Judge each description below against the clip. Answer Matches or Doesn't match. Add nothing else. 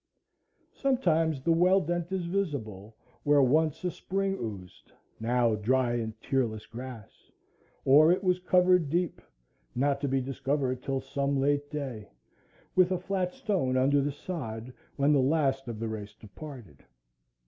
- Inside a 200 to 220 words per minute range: Doesn't match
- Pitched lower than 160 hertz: Matches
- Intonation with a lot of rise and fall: Matches